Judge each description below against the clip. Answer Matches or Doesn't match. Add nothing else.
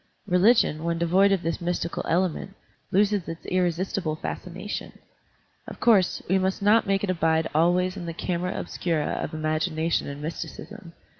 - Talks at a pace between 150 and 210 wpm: Matches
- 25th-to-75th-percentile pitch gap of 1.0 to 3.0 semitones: Matches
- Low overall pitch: Doesn't match